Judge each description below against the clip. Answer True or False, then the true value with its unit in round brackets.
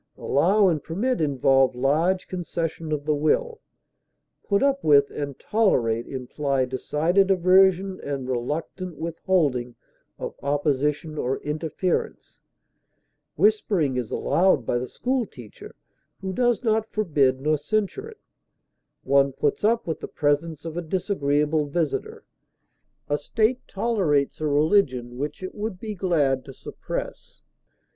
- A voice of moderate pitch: True (155 Hz)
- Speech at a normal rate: False (130 wpm)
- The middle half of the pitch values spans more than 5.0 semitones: True (5.5 semitones)